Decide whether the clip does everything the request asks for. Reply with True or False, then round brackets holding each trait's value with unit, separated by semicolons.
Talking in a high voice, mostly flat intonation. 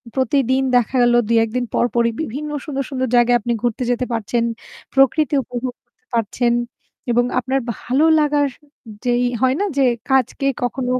True (250 Hz; 2.1 semitones)